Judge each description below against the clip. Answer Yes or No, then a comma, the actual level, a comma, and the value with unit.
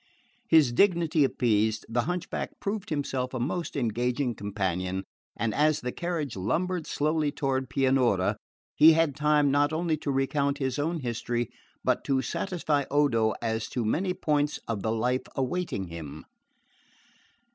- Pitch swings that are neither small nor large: Yes, average, 4.9 semitones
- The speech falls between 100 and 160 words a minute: Yes, average, 145 wpm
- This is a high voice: No, low, 135 Hz